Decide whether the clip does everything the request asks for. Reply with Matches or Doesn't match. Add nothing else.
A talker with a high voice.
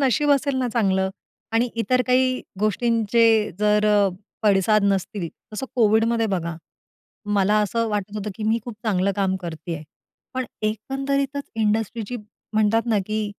Matches